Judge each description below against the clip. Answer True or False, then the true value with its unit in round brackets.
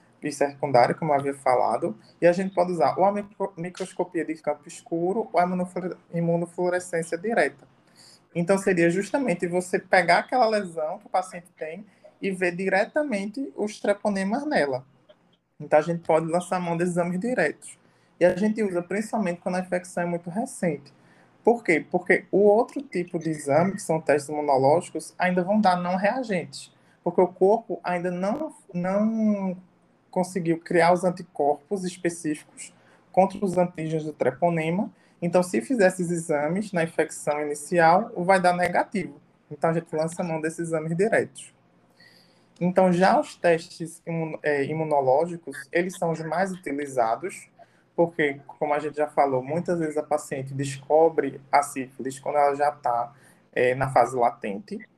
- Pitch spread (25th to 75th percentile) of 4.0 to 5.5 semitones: False (3.5 semitones)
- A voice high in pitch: False (175 Hz)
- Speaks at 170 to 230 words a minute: False (155 wpm)